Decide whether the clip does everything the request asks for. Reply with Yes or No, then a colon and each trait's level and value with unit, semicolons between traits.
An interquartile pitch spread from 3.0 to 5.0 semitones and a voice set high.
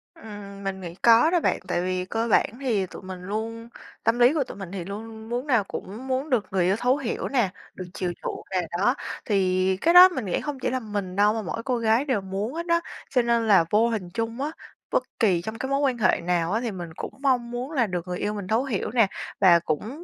Yes: average, 4.6 semitones; high, 220 Hz